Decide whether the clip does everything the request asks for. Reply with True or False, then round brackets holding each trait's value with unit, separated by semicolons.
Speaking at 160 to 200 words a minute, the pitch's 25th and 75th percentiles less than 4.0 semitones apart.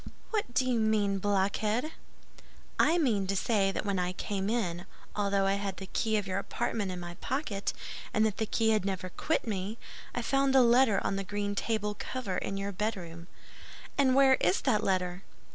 True (190 wpm; 3.2 semitones)